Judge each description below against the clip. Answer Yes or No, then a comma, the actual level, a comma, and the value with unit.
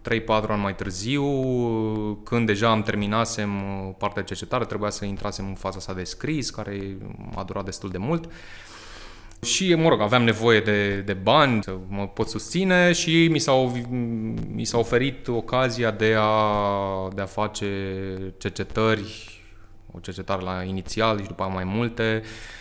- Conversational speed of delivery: Yes, average, 155 wpm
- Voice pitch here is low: Yes, low, 105 Hz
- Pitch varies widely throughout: No, average, 3.0 semitones